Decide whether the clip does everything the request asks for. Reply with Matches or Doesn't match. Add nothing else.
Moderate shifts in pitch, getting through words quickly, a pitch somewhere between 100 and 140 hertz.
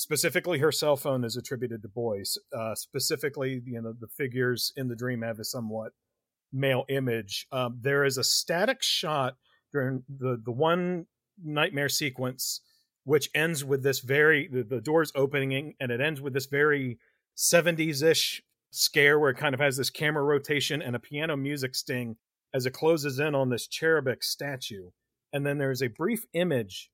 Doesn't match